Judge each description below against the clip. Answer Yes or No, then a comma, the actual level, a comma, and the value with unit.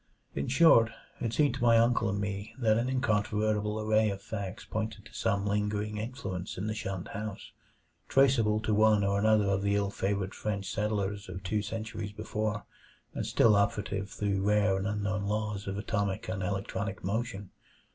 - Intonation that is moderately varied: No, narrow, 1.5 semitones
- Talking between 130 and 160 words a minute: No, average, 175 wpm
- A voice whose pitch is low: Yes, low, 105 Hz